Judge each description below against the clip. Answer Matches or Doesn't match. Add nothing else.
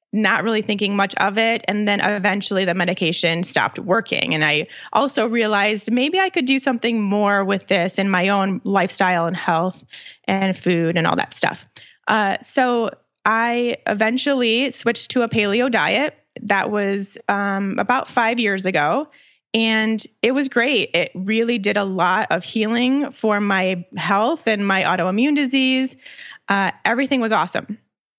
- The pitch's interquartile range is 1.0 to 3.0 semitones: Doesn't match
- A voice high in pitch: Matches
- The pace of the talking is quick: Doesn't match